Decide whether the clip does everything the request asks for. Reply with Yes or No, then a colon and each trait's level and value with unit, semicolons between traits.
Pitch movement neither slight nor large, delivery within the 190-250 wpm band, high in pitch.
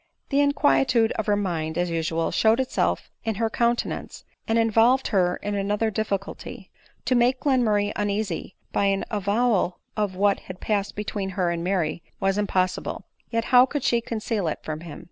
No: average, 3.7 semitones; average, 175 wpm; high, 205 Hz